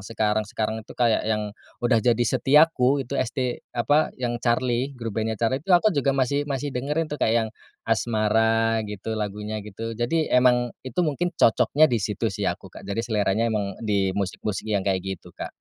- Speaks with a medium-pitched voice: No, low, 115 Hz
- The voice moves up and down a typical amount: Yes, average, 3.7 semitones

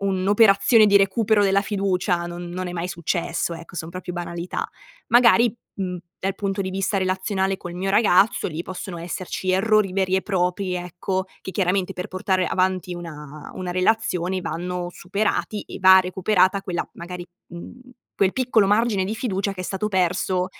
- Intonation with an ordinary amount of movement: No, narrow, 1.8 semitones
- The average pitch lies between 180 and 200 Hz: Yes, medium, 185 Hz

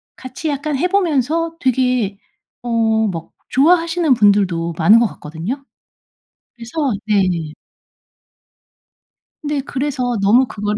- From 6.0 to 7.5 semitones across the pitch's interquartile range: Yes, wide, 6.5 semitones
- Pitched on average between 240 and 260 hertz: Yes, very high, 250 Hz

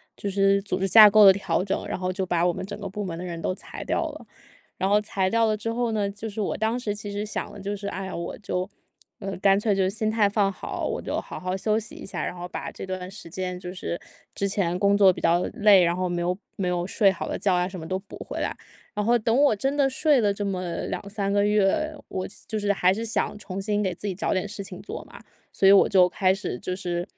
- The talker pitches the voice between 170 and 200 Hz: Yes, high, 195 Hz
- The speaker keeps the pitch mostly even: Yes, narrow, 2.2 semitones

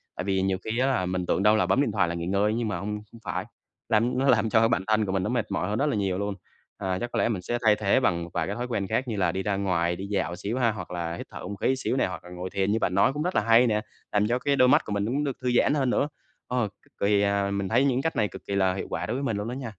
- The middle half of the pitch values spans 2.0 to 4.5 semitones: Yes, average, 4.1 semitones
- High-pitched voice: No, low, 105 Hz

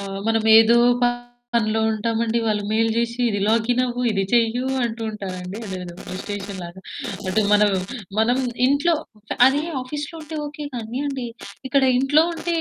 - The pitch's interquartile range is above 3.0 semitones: Yes, average, 3.5 semitones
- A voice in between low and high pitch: No, high, 225 Hz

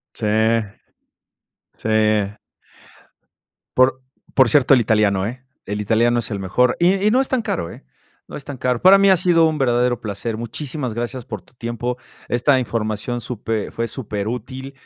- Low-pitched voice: Yes, low, 120 Hz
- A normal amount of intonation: Yes, average, 3.4 semitones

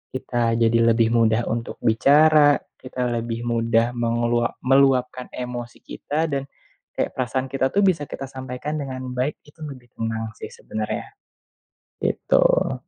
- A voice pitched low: Yes, low, 125 Hz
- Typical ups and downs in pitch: Yes, average, 3.0 semitones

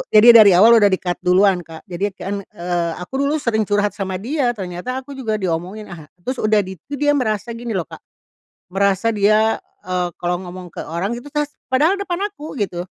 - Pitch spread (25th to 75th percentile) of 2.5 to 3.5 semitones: No, average, 5.0 semitones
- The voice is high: Yes, high, 205 Hz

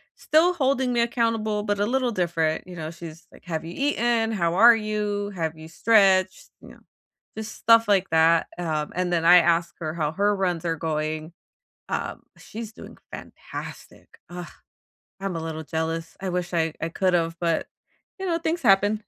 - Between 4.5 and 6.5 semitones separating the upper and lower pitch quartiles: Yes, average, 4.9 semitones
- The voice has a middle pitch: Yes, medium, 180 Hz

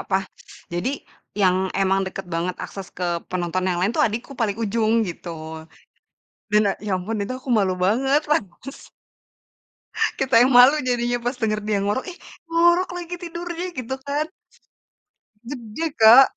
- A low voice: No, high, 230 Hz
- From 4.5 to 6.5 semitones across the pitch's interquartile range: Yes, wide, 5.5 semitones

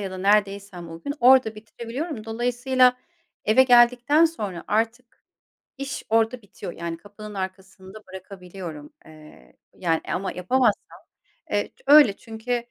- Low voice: No, high, 215 Hz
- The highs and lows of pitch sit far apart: No, average, 4.6 semitones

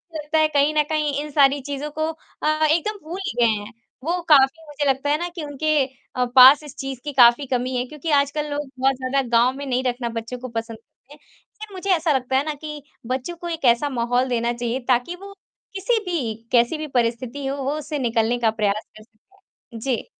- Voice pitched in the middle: No, very high, 275 Hz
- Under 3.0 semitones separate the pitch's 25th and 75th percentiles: No, average, 3.9 semitones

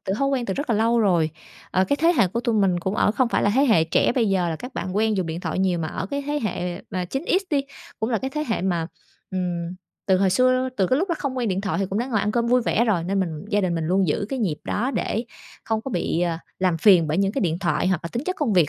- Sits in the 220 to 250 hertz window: No, high, 200 Hz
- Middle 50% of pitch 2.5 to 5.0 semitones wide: No, wide, 5.4 semitones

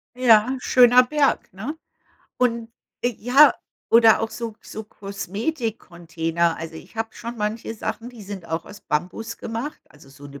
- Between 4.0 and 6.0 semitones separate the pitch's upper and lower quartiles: Yes, average, 5.1 semitones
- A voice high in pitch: Yes, high, 225 Hz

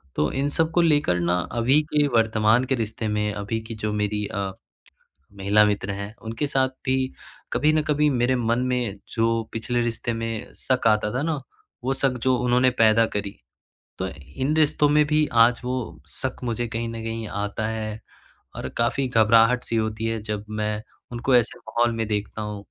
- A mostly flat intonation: No, average, 3.0 semitones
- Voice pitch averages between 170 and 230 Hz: No, low, 115 Hz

